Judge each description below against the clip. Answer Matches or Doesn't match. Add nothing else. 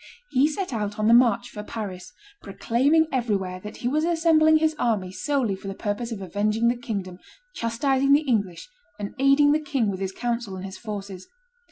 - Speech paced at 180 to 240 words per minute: Matches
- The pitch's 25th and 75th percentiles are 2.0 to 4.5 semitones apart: Doesn't match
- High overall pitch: Matches